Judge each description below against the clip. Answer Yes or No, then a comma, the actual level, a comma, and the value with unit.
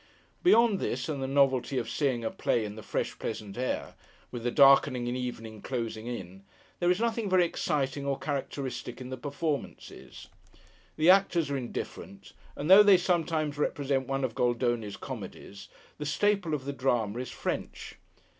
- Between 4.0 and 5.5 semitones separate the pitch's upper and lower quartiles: Yes, average, 4.5 semitones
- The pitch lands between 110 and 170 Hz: Yes, low, 135 Hz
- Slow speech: No, average, 165 wpm